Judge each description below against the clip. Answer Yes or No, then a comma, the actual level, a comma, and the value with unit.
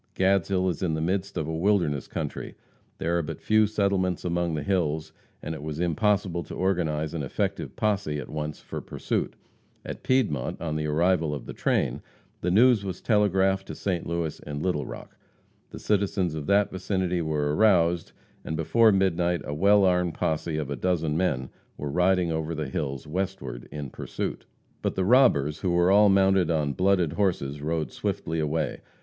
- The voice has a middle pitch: No, very low, 85 Hz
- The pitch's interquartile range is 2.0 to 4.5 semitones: Yes, average, 3.9 semitones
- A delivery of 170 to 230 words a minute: Yes, average, 180 wpm